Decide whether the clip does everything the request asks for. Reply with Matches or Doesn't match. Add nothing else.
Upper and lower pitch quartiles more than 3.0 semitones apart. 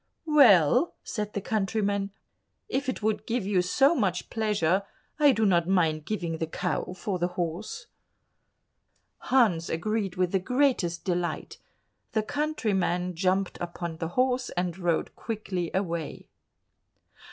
Matches